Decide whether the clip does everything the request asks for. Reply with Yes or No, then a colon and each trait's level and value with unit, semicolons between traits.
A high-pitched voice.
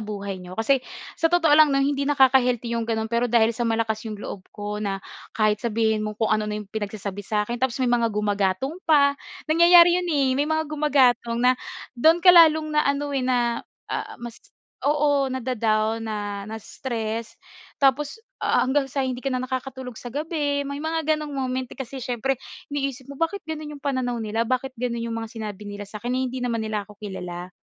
Yes: high, 245 Hz